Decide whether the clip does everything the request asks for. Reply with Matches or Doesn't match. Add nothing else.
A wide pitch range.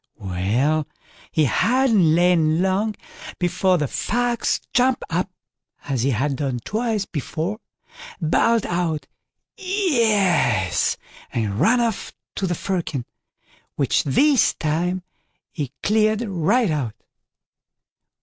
Matches